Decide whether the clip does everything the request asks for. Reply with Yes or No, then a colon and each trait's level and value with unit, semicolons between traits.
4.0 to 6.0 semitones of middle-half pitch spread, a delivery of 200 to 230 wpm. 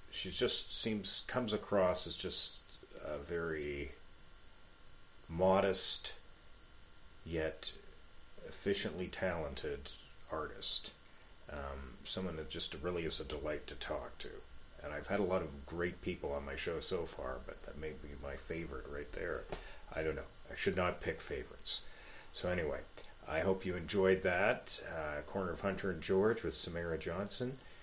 No: average, 4.4 semitones; average, 150 wpm